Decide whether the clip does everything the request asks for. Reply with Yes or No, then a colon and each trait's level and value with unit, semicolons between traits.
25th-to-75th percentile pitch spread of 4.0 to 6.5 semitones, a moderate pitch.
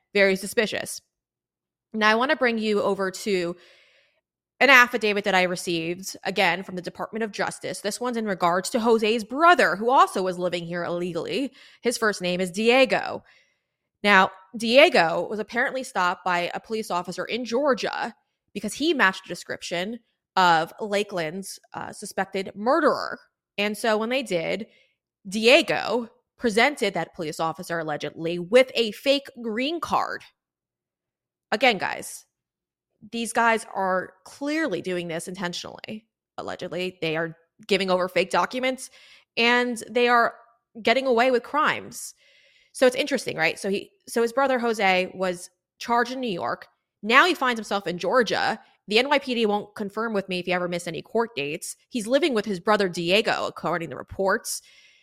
No: average, 4.8 semitones; high, 210 Hz